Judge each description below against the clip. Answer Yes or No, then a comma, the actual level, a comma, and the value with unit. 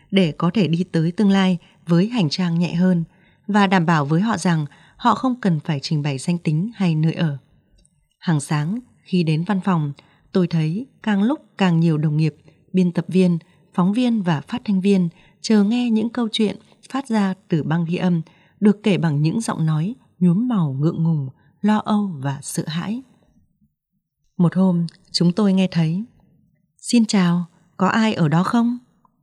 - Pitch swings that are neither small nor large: Yes, average, 3.9 semitones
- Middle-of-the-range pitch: Yes, medium, 180 Hz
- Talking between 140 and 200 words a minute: Yes, average, 185 wpm